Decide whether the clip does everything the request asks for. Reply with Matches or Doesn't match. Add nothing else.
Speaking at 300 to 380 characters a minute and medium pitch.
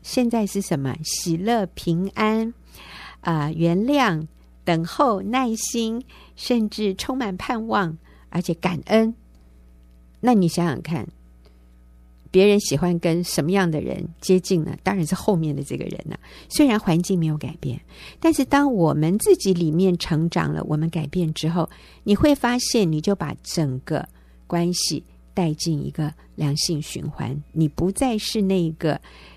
Doesn't match